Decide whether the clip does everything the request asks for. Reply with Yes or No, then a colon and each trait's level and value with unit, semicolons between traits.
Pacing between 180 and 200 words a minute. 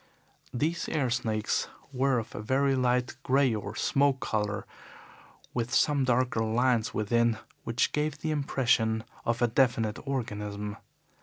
No: slow, 135 wpm